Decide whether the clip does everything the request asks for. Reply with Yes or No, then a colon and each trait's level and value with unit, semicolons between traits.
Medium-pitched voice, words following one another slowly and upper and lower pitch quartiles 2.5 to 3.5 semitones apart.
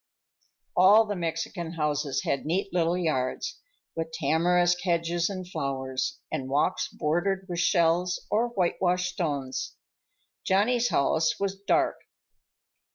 Yes: medium, 175 Hz; slow, 115 wpm; average, 2.9 semitones